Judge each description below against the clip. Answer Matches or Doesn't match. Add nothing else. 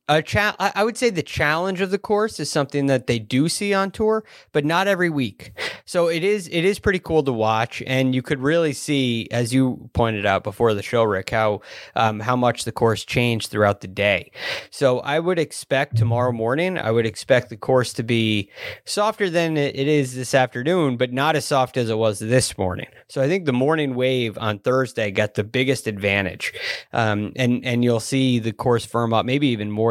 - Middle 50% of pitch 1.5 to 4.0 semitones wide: Doesn't match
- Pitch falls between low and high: Doesn't match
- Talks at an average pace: Doesn't match